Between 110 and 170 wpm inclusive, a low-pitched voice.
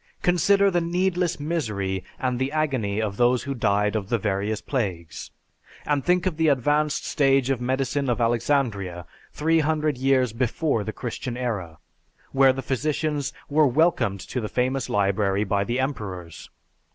Yes: average, 155 wpm; low, 130 Hz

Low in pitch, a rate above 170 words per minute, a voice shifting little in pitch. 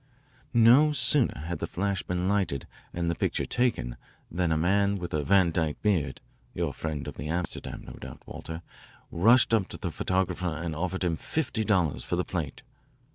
No: very low, 90 Hz; average, 185 wpm; average, 3.8 semitones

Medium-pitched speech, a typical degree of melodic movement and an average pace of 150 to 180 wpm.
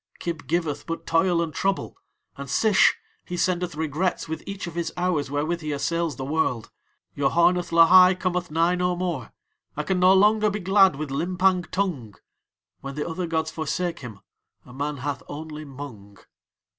Yes: medium, 165 Hz; average, 3.9 semitones; average, 170 wpm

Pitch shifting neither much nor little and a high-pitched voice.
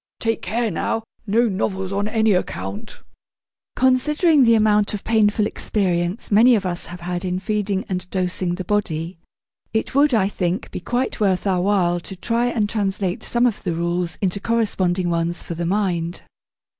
Yes: average, 3.7 semitones; high, 195 Hz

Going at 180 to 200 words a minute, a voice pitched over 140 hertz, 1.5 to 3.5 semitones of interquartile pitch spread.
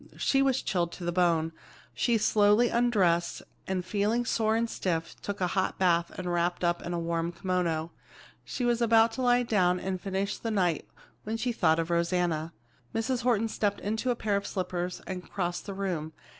No: average, 190 wpm; high, 190 Hz; average, 4.5 semitones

